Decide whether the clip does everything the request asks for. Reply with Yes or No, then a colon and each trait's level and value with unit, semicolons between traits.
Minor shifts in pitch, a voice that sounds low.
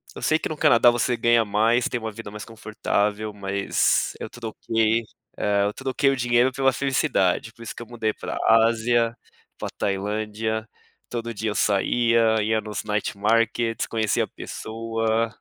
Yes: narrow, 1.8 semitones; low, 115 Hz